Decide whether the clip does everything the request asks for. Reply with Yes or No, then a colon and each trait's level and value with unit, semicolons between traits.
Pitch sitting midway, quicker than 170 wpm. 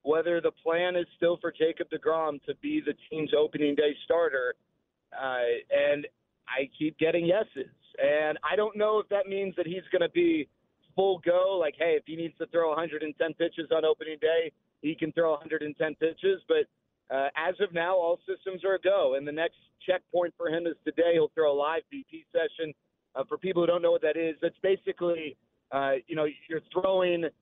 Yes: medium, 170 Hz; average, 200 wpm